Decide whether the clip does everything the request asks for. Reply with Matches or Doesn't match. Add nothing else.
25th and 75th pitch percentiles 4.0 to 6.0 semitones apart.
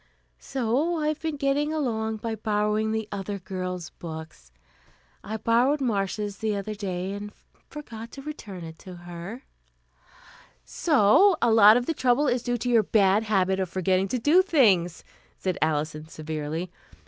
Matches